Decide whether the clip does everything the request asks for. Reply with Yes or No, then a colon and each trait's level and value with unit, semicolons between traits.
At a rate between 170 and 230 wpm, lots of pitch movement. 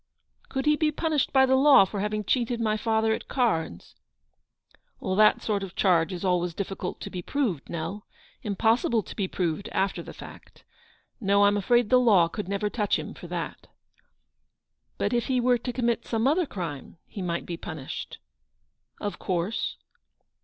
No: average, 190 wpm; average, 4.7 semitones